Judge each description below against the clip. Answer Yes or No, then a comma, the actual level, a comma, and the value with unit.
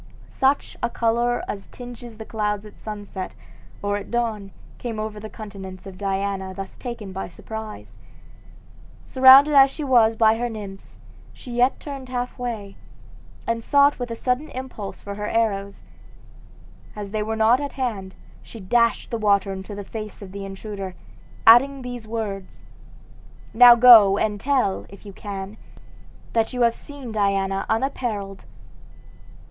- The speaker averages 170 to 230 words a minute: No, average, 155 wpm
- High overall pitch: Yes, high, 220 Hz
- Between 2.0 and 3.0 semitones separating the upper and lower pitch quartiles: No, average, 3.4 semitones